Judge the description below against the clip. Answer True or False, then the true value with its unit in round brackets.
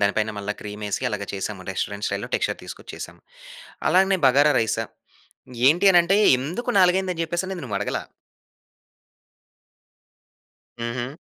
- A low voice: True (130 Hz)